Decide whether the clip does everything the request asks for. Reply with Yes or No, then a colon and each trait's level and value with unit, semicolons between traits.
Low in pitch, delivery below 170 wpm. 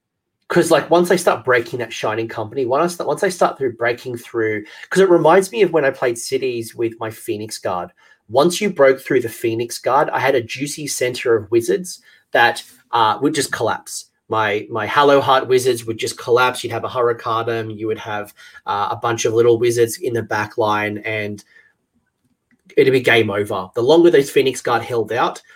No: low, 125 Hz; fast, 205 wpm